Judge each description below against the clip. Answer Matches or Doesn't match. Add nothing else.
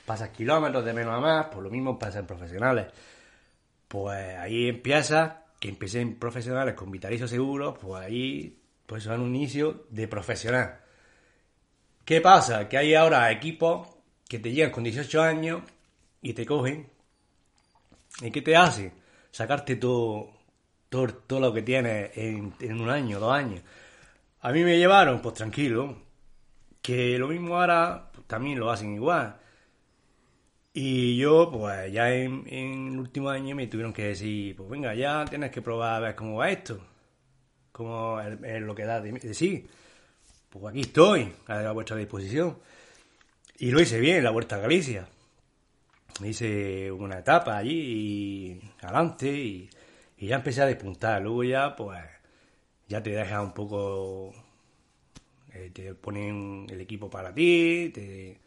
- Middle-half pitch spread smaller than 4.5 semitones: Doesn't match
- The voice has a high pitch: Doesn't match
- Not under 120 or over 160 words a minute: Matches